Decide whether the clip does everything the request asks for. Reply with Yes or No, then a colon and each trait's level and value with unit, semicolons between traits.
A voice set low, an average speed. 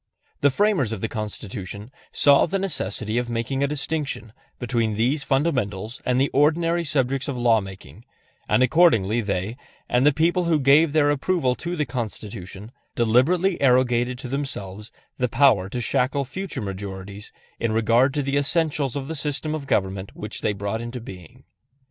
Yes: low, 125 Hz; average, 165 wpm